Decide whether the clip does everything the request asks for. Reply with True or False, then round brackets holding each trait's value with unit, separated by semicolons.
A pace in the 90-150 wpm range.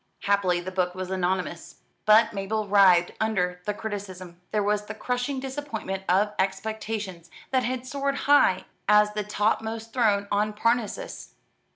True (145 wpm)